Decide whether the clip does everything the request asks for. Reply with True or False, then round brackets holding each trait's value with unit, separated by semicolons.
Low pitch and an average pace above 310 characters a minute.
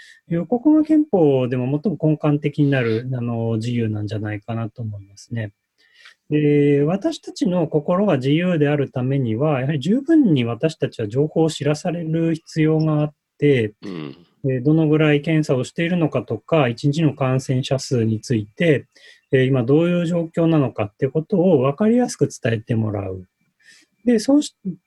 False (145 Hz; 325 characters per minute)